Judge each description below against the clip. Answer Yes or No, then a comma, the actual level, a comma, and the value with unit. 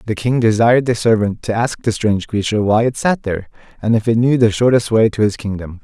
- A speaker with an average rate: No, fast, 245 wpm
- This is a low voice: Yes, low, 110 Hz